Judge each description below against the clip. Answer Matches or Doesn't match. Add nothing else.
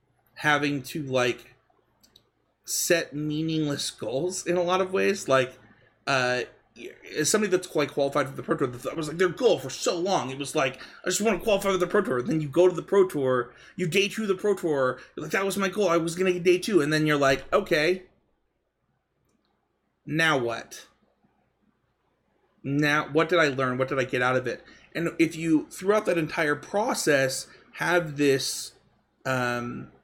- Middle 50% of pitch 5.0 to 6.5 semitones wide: Matches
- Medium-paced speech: Matches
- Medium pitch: Matches